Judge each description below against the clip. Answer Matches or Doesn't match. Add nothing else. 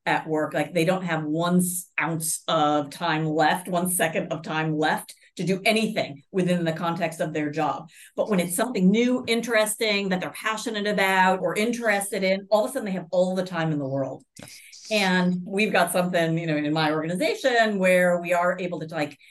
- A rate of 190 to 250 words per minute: Matches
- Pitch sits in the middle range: Matches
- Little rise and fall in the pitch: Doesn't match